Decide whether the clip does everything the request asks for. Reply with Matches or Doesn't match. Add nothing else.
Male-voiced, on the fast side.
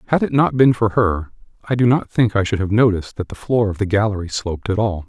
Matches